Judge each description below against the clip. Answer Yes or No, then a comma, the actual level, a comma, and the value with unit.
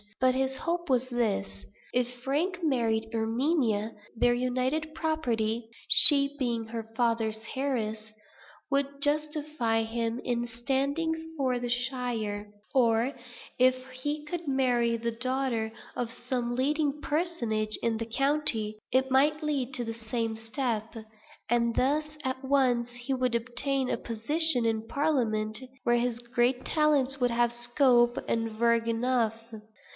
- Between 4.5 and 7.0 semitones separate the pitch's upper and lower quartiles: No, average, 3.3 semitones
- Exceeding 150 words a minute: No, slow, 135 wpm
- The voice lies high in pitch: Yes, high, 245 Hz